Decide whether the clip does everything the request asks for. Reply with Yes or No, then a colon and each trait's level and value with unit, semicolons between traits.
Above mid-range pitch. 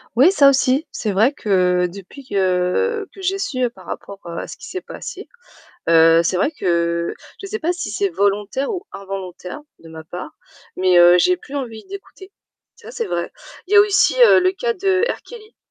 Yes: very high, 255 Hz